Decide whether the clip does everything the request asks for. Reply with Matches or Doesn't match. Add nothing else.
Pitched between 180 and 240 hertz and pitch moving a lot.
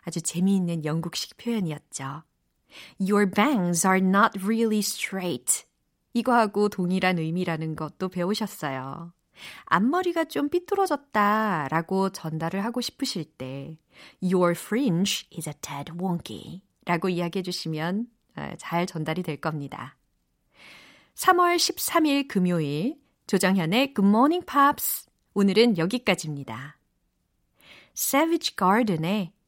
Matches